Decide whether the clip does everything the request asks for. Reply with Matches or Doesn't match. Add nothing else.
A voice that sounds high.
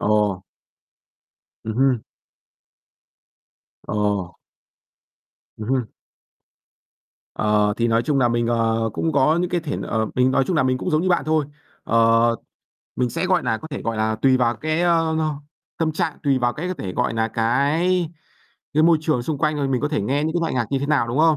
Doesn't match